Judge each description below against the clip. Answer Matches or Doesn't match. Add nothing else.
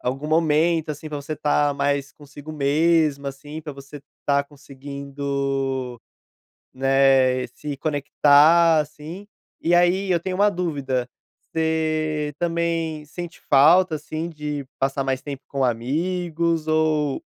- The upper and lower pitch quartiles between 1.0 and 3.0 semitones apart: Matches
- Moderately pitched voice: Matches